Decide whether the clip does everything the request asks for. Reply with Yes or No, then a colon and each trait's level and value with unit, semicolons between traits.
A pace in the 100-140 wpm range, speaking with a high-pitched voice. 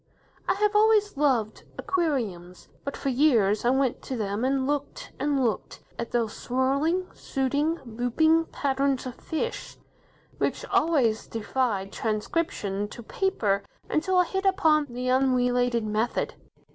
Yes: slow, 135 wpm; very high, 260 Hz